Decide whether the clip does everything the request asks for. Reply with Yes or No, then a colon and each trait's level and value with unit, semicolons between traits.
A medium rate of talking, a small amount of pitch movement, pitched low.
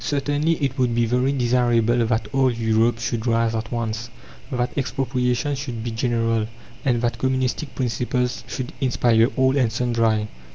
Yes: average, 155 wpm; narrow, 2.2 semitones; low, 120 Hz